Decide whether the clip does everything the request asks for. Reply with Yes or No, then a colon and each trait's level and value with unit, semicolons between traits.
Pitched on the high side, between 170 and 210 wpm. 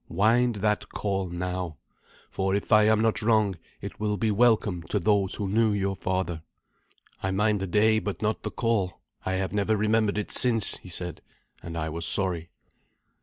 No: low, 100 Hz; average, 180 wpm